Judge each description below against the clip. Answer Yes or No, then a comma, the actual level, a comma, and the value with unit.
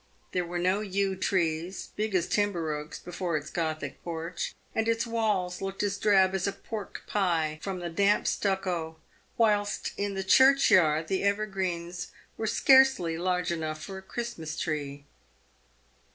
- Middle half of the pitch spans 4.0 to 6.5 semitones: No, average, 3.5 semitones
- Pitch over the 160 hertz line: Yes, medium, 185 Hz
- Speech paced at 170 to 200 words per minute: No, average, 155 wpm